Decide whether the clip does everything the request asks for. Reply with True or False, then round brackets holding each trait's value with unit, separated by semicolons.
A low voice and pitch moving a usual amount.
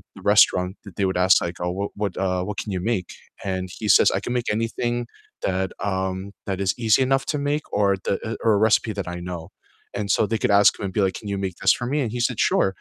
True (100 Hz; 3.2 semitones)